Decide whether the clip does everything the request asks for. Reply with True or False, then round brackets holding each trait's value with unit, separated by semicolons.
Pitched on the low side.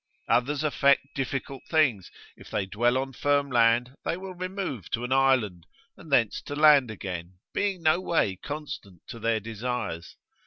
True (130 Hz)